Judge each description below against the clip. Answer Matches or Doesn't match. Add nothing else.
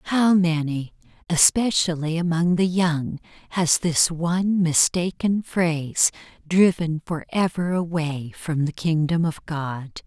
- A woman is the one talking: Matches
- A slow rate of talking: Matches